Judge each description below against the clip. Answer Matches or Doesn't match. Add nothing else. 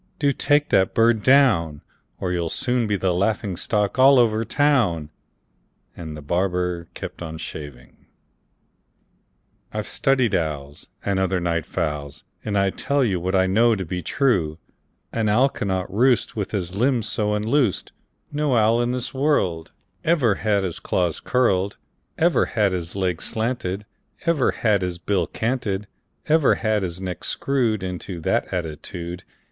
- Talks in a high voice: Doesn't match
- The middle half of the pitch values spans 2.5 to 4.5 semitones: Doesn't match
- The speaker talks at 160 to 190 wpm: Doesn't match